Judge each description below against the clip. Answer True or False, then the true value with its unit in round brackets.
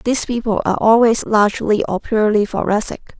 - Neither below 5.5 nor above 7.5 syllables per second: True (5.9 syllables/s)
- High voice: True (215 Hz)